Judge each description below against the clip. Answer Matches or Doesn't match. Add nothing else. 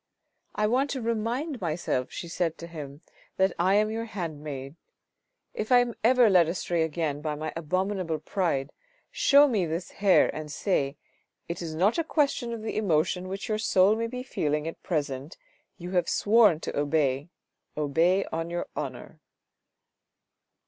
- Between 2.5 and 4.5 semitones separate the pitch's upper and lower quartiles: Doesn't match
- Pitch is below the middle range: Doesn't match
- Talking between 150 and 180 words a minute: Matches